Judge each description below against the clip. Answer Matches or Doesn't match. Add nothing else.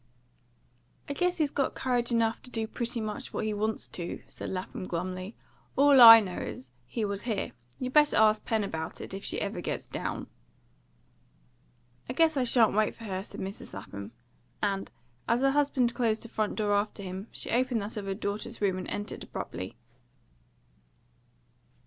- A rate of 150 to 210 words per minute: Matches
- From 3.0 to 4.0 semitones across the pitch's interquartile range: Matches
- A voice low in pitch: Doesn't match